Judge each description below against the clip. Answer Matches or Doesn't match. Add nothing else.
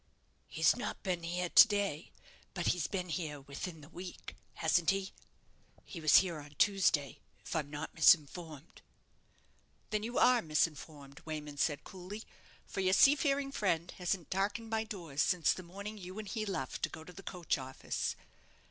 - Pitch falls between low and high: Matches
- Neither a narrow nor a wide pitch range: Matches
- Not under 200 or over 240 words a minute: Doesn't match